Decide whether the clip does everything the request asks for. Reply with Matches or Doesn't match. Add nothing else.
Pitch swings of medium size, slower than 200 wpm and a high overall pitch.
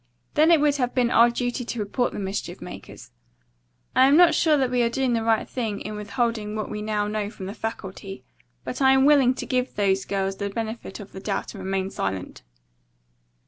Doesn't match